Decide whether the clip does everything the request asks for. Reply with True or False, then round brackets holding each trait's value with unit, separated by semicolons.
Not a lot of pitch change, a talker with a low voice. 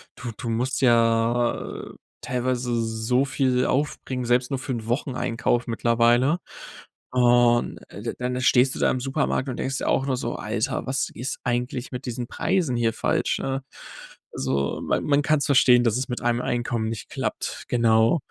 True (1.8 semitones; 125 Hz)